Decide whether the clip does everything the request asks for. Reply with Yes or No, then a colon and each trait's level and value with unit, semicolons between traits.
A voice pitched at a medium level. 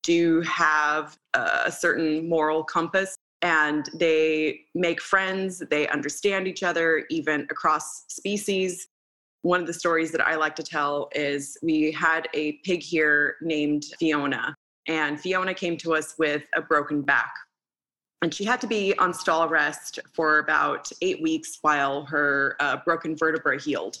Yes: medium, 160 Hz